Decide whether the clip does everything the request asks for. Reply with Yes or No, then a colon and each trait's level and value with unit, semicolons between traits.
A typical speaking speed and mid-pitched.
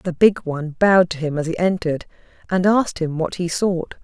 No: fast, 225 wpm; medium, 175 Hz